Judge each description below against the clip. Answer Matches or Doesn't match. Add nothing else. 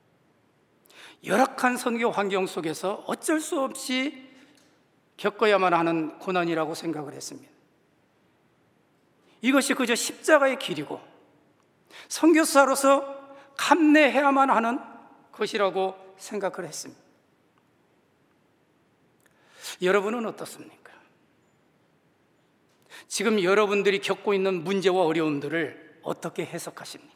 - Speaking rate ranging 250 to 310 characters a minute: Doesn't match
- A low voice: Doesn't match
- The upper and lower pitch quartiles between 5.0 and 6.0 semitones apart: Doesn't match